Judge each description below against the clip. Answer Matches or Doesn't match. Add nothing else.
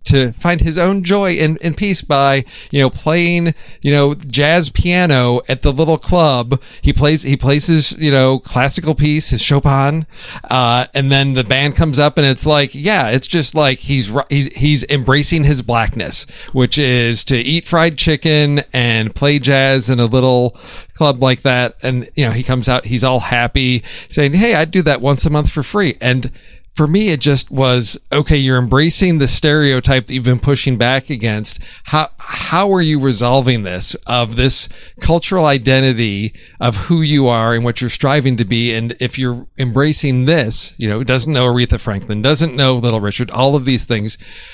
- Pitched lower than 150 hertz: Matches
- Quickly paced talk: Doesn't match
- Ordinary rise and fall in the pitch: Matches